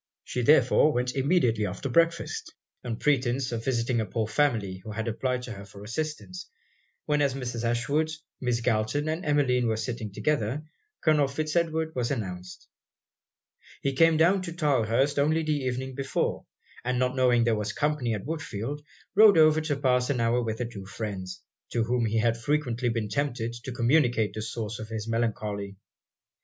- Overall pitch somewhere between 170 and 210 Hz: No, low, 125 Hz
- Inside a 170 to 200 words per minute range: Yes, average, 175 wpm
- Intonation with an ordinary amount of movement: Yes, average, 4.6 semitones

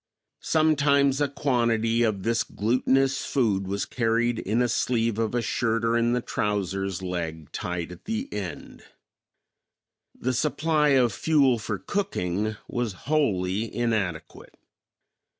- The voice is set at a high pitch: No, low, 115 Hz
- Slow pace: Yes, slow, 130 wpm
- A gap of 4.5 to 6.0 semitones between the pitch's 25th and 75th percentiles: Yes, average, 5.1 semitones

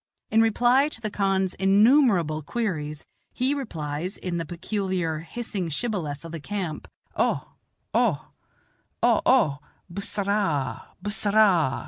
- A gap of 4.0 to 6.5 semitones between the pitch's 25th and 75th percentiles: Yes, average, 5.3 semitones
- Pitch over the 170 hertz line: Yes, high, 190 Hz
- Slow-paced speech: No, average, 150 wpm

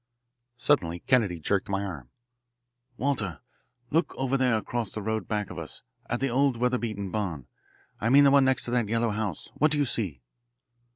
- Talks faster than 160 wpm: Yes, average, 180 wpm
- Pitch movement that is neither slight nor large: Yes, average, 4.8 semitones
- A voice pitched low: Yes, low, 115 Hz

